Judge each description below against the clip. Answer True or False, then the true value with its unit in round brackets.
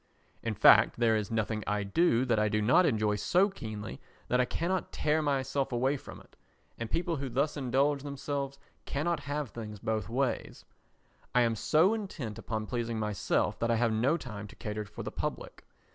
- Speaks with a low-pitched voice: True (120 Hz)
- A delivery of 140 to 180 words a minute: False (190 wpm)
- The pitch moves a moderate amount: True (4.8 semitones)